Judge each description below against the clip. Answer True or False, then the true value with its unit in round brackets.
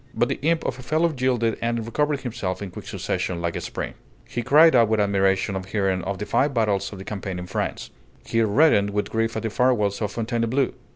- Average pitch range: True (4.2 semitones)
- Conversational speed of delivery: False (225 wpm)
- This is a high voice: False (110 Hz)